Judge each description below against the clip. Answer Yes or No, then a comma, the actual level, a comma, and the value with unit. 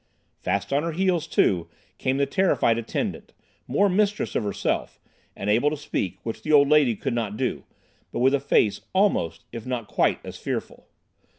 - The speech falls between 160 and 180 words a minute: Yes, average, 170 wpm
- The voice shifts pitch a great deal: Yes, wide, 5.9 semitones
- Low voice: Yes, low, 130 Hz